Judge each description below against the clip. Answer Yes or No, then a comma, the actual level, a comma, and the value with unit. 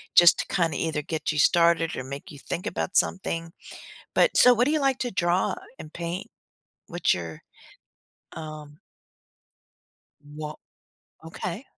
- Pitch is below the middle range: No, medium, 165 Hz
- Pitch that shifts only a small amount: No, average, 3.3 semitones